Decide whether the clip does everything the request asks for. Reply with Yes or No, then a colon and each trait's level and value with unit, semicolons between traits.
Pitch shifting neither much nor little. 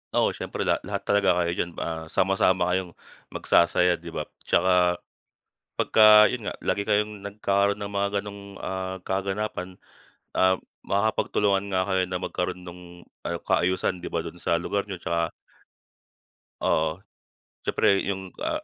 No: narrow, 2.3 semitones